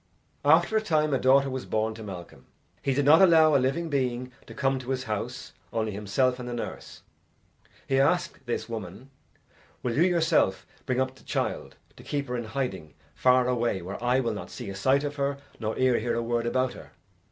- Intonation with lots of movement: No, average, 3.2 semitones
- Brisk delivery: Yes, fast, 210 wpm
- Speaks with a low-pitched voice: Yes, low, 130 Hz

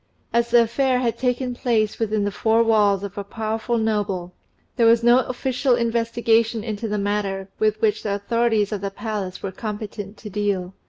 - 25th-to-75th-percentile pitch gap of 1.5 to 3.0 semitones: Yes, narrow, 2.5 semitones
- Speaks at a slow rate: No, average, 180 wpm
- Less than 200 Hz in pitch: No, high, 220 Hz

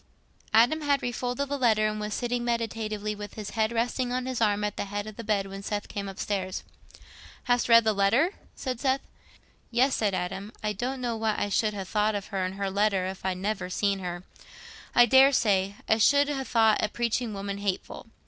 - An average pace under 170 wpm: No, fast, 205 wpm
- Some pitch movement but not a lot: Yes, average, 3.3 semitones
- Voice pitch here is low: No, high, 215 Hz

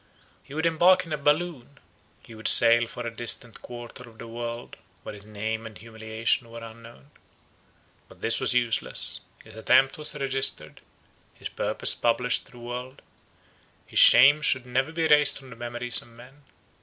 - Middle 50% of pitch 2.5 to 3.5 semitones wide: Yes, average, 3.0 semitones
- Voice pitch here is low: Yes, low, 120 Hz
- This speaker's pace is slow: No, average, 170 wpm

